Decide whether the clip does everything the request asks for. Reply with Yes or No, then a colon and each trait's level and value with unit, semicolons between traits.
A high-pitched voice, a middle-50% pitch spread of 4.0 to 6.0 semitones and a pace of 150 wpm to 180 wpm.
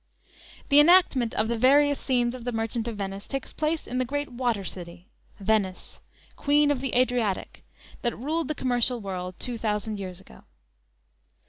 Yes: high, 240 Hz; average, 4.6 semitones; average, 165 wpm